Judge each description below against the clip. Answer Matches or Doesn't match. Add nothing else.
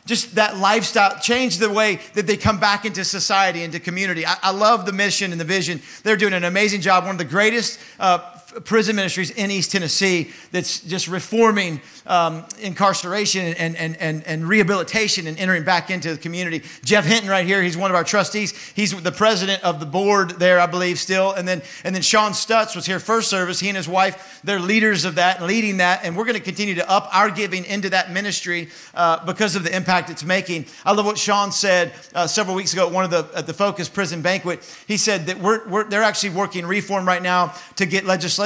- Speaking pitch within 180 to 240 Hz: Matches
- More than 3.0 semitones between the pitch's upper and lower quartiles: Doesn't match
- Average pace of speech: Doesn't match